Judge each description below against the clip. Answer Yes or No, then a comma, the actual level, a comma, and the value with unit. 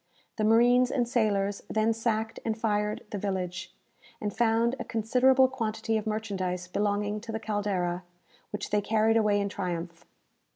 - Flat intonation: Yes, narrow, 2.0 semitones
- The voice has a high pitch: Yes, high, 215 Hz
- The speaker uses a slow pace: No, average, 155 wpm